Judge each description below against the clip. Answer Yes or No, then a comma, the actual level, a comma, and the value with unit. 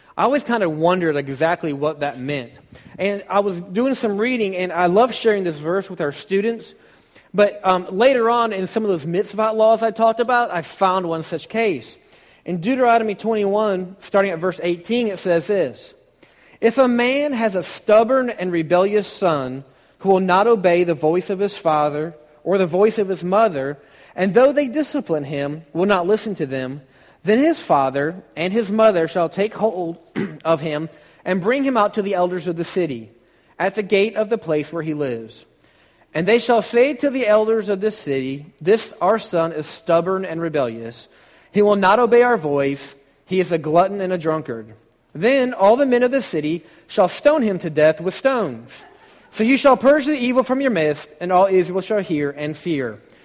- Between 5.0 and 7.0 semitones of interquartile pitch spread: Yes, wide, 5.5 semitones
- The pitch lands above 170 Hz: Yes, high, 190 Hz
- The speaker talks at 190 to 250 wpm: Yes, average, 200 wpm